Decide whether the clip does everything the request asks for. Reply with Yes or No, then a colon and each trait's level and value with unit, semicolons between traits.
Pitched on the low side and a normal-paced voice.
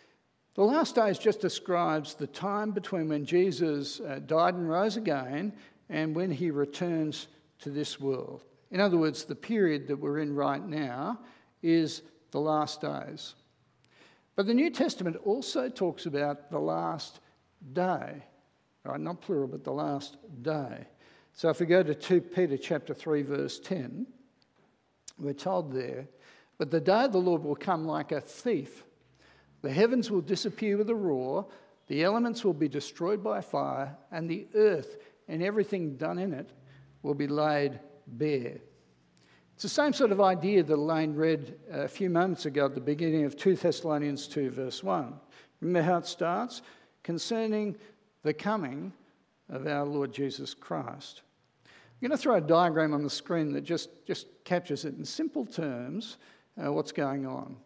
No: medium, 165 Hz; average, 165 wpm